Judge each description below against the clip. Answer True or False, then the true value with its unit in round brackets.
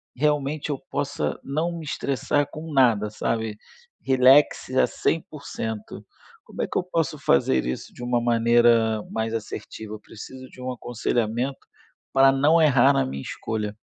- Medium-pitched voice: False (130 Hz)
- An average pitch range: True (4.3 semitones)